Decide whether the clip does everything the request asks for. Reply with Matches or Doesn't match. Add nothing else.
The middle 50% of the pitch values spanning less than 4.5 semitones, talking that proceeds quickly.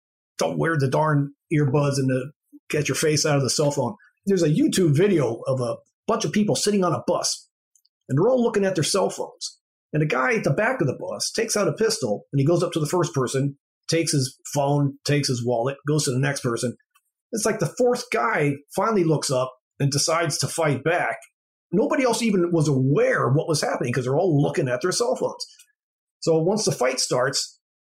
Doesn't match